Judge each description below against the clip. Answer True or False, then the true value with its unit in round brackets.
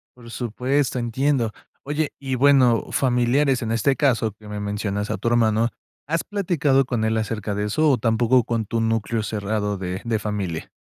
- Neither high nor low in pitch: False (115 Hz)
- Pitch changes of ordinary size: True (3.7 semitones)